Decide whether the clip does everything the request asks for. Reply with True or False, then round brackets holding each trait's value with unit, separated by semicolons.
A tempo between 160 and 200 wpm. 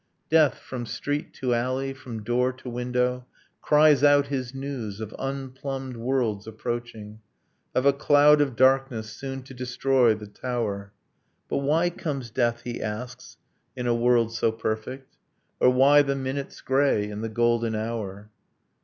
False (150 wpm)